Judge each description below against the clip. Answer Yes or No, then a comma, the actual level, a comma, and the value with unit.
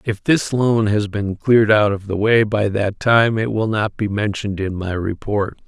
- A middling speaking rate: No, fast, 220 wpm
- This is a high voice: No, low, 105 Hz